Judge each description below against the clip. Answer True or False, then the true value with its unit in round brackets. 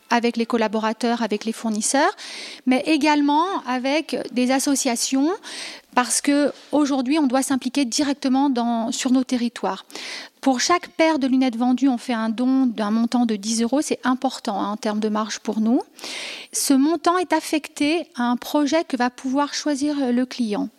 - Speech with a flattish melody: False (3.7 semitones)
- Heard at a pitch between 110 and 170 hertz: False (265 Hz)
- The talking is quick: False (165 wpm)